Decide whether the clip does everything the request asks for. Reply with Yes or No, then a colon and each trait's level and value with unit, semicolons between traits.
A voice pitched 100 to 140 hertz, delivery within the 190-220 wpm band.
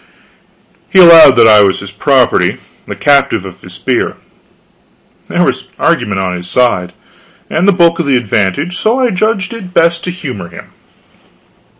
No: low, 135 Hz; average, 165 wpm